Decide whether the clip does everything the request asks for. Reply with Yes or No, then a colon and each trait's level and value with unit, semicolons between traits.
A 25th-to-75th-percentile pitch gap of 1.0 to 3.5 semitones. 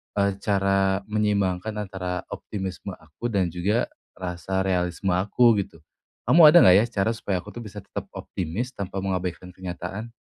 Yes: narrow, 2.5 semitones